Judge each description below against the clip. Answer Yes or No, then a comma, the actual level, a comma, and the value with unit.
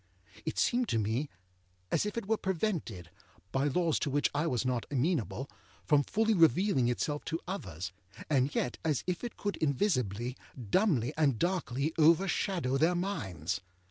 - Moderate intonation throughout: No, wide, 6.6 semitones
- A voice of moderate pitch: Yes, medium, 150 Hz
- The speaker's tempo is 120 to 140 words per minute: No, average, 155 wpm